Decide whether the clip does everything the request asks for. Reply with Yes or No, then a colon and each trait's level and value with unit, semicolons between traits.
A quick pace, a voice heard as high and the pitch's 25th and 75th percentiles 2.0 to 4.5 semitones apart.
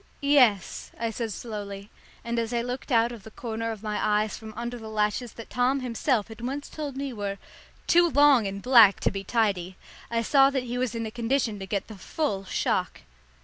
Yes: fast, 210 wpm; high, 230 Hz; average, 3.0 semitones